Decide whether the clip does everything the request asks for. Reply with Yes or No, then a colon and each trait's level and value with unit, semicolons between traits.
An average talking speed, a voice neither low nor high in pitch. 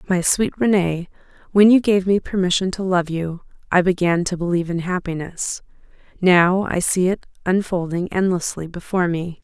Yes: average, 155 wpm; medium, 180 Hz